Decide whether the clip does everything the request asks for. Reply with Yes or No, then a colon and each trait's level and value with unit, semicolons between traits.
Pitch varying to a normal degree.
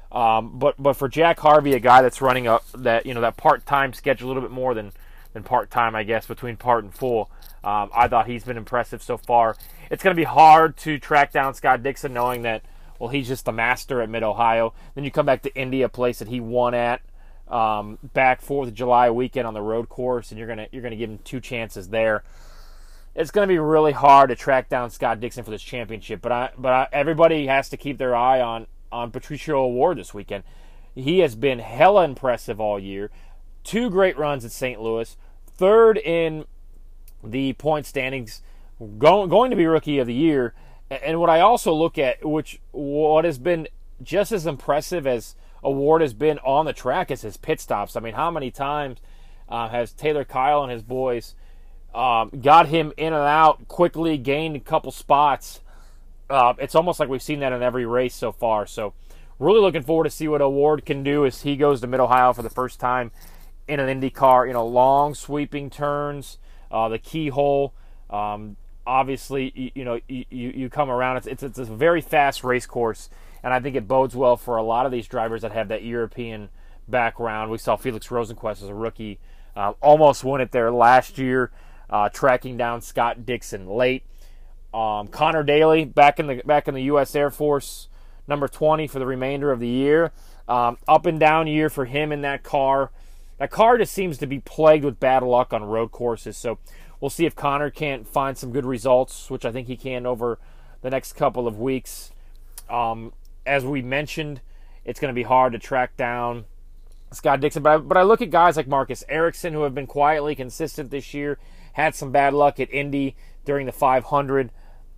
Yes: average, 4.1 semitones